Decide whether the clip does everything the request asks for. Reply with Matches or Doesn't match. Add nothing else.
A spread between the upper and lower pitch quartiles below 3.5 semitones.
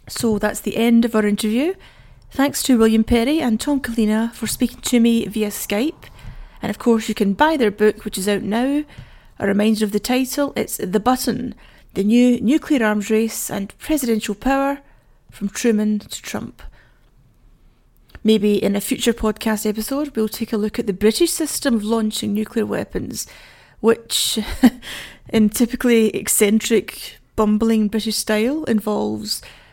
Matches